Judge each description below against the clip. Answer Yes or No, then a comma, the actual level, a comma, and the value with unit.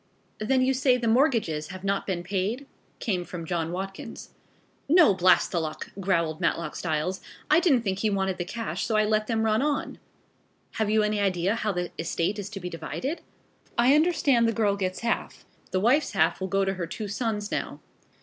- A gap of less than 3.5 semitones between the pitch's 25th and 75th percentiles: No, average, 4.1 semitones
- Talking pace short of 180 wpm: No, average, 200 wpm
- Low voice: No, high, 205 Hz